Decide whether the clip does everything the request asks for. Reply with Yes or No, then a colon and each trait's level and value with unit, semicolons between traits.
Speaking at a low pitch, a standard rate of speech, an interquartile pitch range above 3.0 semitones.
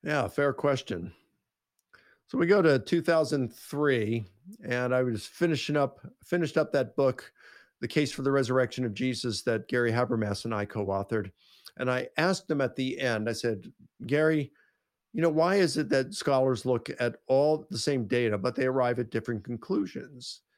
Yes: low, 130 Hz; average, 170 wpm; average, 3.8 semitones